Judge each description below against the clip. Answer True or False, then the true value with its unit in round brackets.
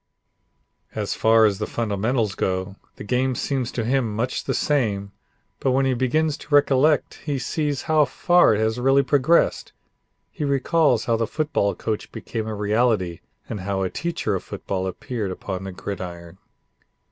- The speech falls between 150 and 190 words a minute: True (165 wpm)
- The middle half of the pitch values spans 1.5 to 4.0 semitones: False (5.3 semitones)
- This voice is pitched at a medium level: False (115 Hz)